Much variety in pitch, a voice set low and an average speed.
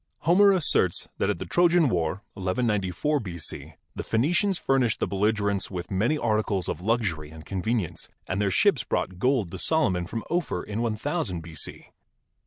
Yes: wide, 6.7 semitones; low, 105 Hz; average, 160 wpm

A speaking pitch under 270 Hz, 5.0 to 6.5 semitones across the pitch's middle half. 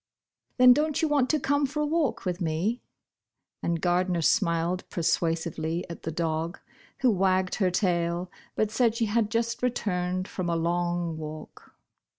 Yes: medium, 185 Hz; wide, 5.6 semitones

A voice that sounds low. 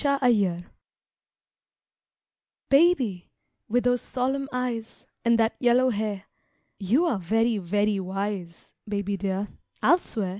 No: high, 220 Hz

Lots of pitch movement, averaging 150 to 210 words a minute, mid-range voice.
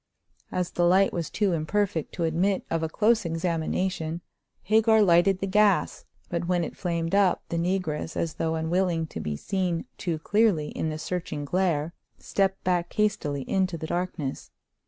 No: average, 2.9 semitones; average, 165 wpm; medium, 175 Hz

